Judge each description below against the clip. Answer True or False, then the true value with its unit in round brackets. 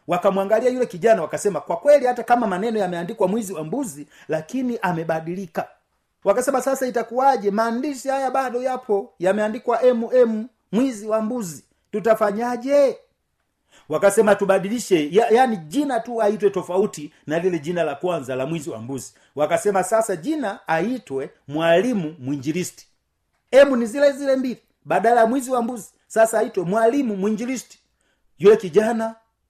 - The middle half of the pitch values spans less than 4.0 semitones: False (5.4 semitones)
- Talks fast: False (115 wpm)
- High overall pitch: True (220 Hz)